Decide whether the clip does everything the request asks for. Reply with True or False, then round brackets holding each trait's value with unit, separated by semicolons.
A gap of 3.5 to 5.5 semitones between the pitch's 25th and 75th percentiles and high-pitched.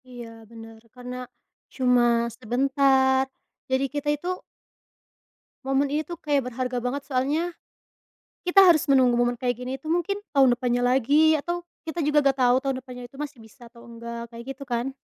False (2.9 semitones; 265 Hz)